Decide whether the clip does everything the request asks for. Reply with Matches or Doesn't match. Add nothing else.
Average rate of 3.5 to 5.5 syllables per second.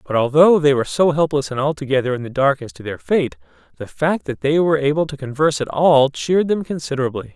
Doesn't match